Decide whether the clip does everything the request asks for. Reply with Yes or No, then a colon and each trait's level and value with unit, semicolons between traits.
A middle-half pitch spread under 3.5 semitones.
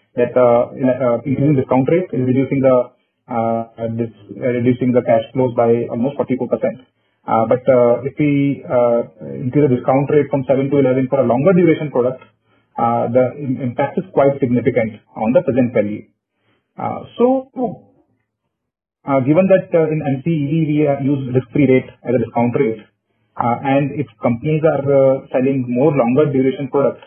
Yes: average, 2.8 semitones